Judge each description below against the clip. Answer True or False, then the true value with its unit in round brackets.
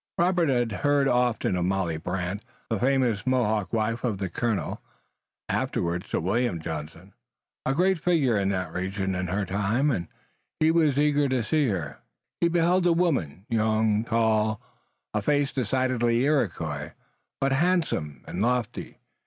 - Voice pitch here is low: True (115 Hz)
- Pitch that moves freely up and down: True (6.4 semitones)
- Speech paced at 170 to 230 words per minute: False (145 wpm)